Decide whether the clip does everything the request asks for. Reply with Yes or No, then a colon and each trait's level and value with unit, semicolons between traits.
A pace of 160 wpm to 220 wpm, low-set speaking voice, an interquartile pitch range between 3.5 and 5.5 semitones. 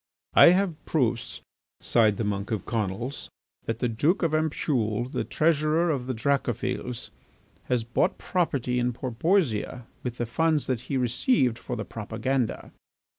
No: average, 145 wpm; low, 125 Hz; average, 5.0 semitones